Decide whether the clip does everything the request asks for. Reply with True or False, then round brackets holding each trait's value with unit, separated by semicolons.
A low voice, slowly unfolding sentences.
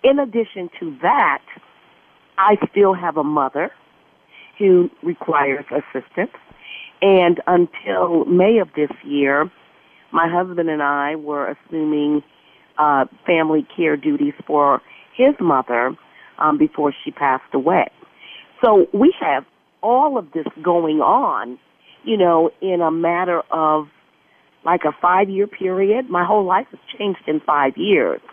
False (175 Hz; 130 wpm)